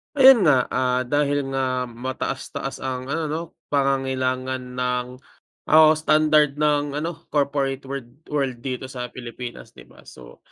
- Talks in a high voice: No, low, 135 Hz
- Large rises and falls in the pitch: No, narrow, 2.6 semitones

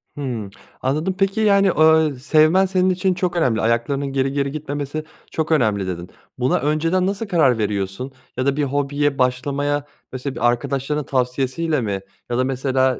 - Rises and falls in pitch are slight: No, average, 3.8 semitones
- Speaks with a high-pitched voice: No, medium, 140 Hz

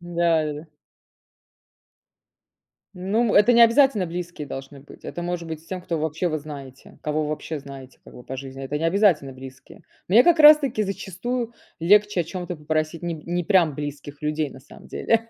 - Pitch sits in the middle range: Yes, medium, 165 Hz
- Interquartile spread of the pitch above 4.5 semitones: Yes, average, 4.9 semitones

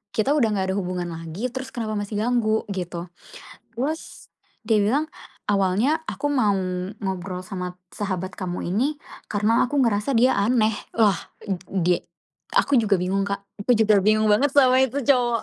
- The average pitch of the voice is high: Yes, high, 215 Hz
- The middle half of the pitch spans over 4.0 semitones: Yes, average, 4.7 semitones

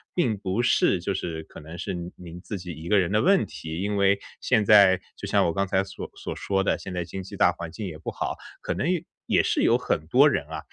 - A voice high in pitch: No, very low, 95 Hz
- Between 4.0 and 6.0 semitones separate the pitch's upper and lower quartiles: No, average, 3.5 semitones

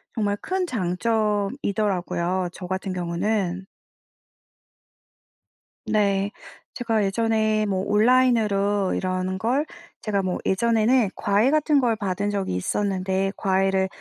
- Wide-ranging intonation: No, average, 2.9 semitones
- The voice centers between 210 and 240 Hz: No, high, 200 Hz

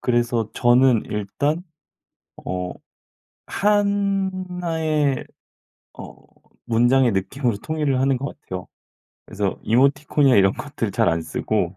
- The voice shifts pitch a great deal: Yes, wide, 6.7 semitones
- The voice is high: No, low, 130 Hz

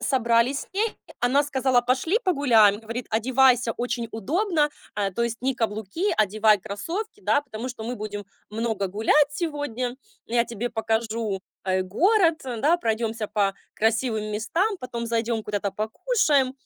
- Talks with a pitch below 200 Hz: No, high, 235 Hz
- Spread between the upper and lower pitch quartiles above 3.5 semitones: Yes, average, 4.5 semitones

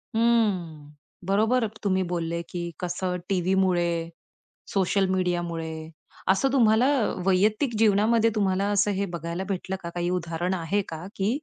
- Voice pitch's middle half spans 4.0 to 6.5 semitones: No, average, 3.3 semitones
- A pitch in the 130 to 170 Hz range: No, high, 190 Hz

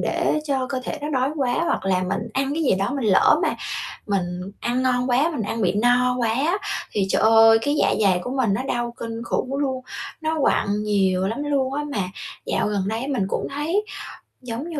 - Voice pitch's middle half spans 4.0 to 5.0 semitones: Yes, average, 4.7 semitones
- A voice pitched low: No, high, 245 Hz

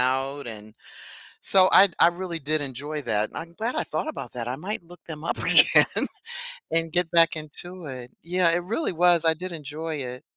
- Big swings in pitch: No, average, 4.4 semitones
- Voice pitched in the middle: Yes, medium, 160 Hz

